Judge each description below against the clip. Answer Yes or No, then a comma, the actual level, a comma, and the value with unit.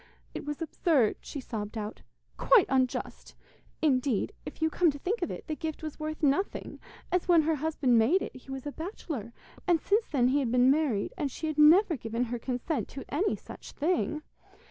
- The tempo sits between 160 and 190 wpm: No, average, 200 wpm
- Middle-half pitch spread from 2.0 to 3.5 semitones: No, average, 4.3 semitones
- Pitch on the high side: Yes, very high, 295 Hz